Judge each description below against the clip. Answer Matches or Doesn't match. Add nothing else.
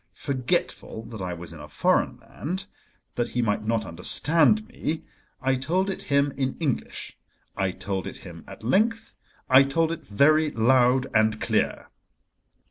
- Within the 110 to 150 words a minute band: Matches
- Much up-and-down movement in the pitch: Matches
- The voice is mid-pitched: Doesn't match